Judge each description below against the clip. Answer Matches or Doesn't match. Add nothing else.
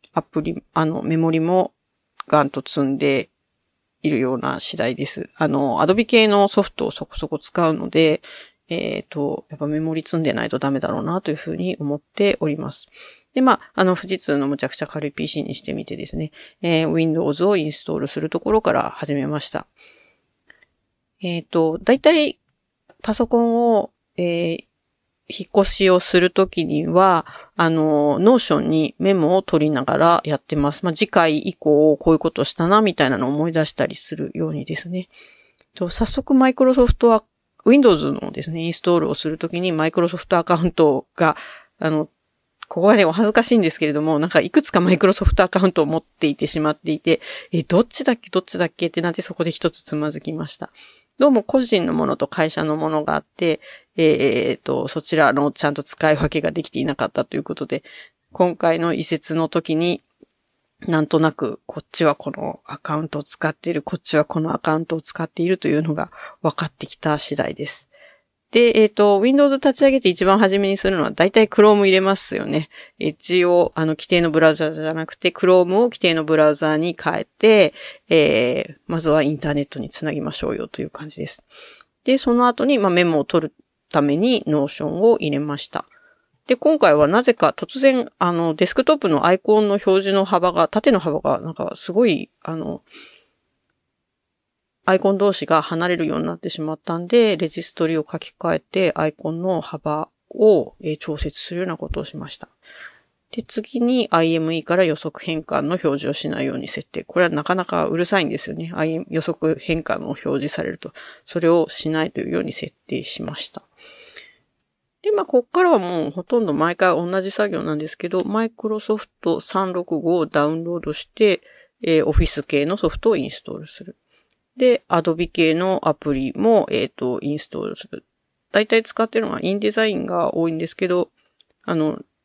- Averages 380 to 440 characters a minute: Matches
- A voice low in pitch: Doesn't match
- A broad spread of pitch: Doesn't match